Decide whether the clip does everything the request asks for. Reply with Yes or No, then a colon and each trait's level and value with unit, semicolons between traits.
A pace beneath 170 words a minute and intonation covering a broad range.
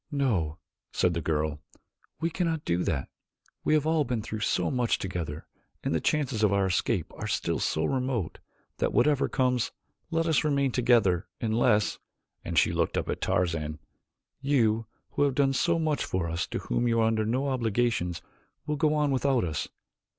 No: average, 180 wpm; wide, 7.4 semitones